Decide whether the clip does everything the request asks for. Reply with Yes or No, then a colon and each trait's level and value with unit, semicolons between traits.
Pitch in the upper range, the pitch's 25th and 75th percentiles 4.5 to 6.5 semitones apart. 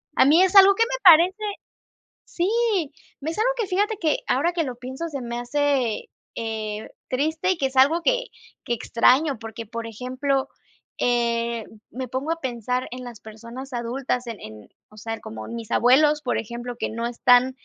Yes: very high, 255 Hz; average, 5.0 semitones